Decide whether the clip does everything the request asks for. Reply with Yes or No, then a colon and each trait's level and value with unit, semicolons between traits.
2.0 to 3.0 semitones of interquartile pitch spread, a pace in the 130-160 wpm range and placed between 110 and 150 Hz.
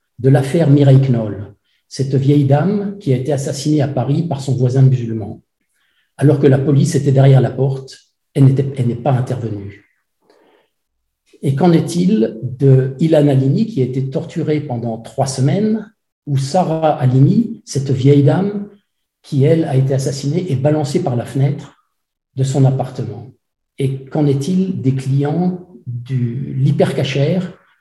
Yes: average, 2.7 semitones; average, 150 wpm; medium, 140 Hz